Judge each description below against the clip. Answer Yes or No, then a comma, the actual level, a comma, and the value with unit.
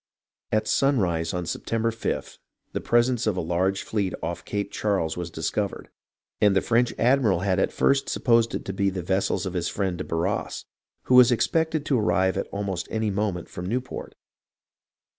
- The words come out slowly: No, average, 175 wpm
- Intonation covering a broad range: No, average, 4.2 semitones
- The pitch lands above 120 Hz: No, low, 100 Hz